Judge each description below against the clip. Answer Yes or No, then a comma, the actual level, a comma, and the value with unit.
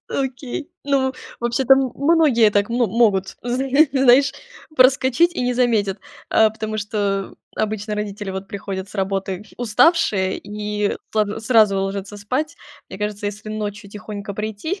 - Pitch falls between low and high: No, high, 215 Hz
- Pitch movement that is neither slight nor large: Yes, average, 3.9 semitones